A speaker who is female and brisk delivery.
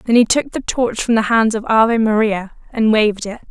Yes: female; fast, 240 wpm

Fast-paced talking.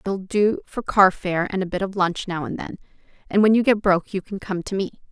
Yes: fast, 270 wpm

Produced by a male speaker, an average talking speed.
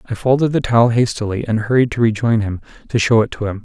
No: male; fast, 245 wpm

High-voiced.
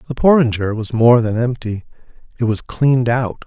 No: low, 120 Hz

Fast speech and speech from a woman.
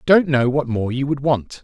No: fast, 295 wpm; male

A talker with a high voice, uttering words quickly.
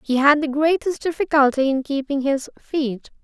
No: very high, 285 Hz; average, 165 wpm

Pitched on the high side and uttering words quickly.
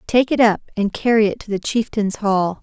Yes: high, 215 Hz; fast, 230 wpm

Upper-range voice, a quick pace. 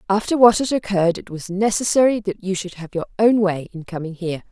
Yes: high, 195 Hz; fast, 225 wpm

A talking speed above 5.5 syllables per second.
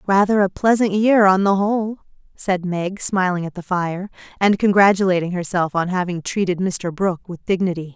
No: 5.1 syllables/s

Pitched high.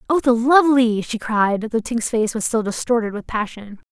Yes: high, 230 Hz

